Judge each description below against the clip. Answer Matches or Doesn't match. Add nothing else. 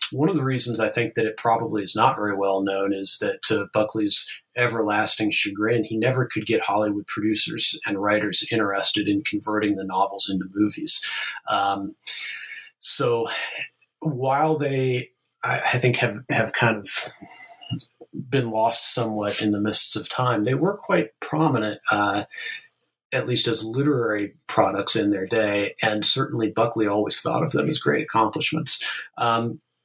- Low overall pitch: Matches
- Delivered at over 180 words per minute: Doesn't match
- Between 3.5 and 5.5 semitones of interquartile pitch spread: Matches